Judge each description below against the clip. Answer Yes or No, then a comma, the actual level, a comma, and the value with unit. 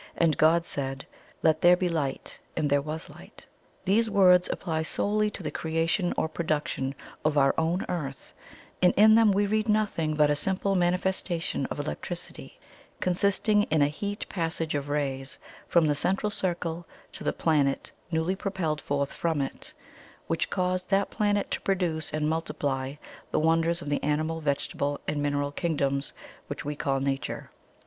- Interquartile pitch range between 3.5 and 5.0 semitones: Yes, average, 4.0 semitones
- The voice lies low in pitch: No, medium, 160 Hz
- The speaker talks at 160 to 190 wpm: Yes, average, 165 wpm